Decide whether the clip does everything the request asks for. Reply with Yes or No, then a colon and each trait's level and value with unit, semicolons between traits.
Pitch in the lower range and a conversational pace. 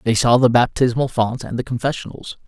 Yes: low, 120 Hz; average, 195 wpm